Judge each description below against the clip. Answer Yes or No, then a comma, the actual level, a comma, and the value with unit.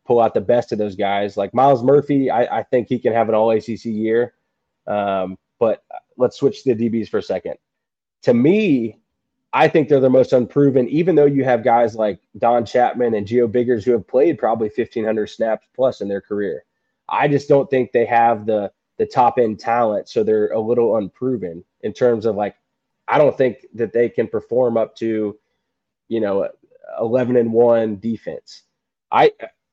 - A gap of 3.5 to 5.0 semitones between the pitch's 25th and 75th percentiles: No, average, 3.1 semitones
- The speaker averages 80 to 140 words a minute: No, average, 195 wpm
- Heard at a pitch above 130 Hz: No, low, 115 Hz